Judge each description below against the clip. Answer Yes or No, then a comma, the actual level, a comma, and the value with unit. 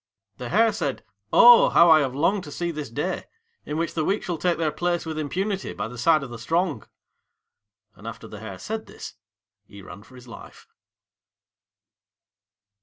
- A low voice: No, medium, 160 Hz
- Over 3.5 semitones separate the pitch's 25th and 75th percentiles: Yes, average, 5.1 semitones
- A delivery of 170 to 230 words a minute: Yes, average, 180 wpm